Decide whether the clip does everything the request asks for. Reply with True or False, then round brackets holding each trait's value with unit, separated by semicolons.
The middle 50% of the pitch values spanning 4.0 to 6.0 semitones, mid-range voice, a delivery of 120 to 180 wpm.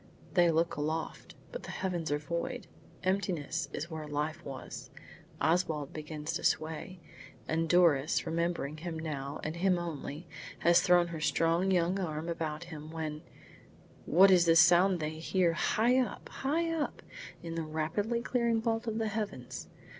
False (3.2 semitones; 170 Hz; 155 wpm)